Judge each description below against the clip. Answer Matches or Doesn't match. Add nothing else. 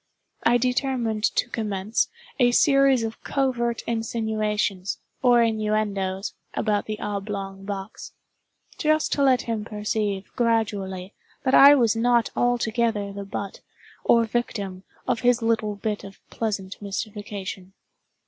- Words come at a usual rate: Doesn't match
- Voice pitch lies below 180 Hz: Doesn't match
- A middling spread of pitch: Matches